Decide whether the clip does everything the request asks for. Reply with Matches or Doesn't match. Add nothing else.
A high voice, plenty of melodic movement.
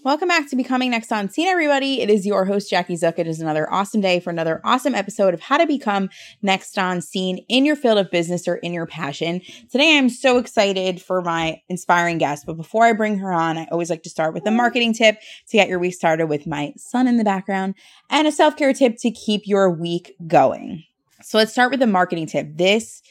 Matches